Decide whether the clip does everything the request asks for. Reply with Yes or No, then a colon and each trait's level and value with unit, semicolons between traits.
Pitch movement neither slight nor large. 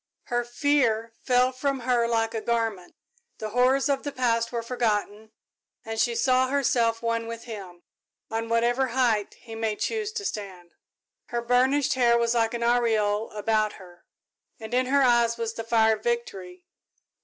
No: narrow, 2.3 semitones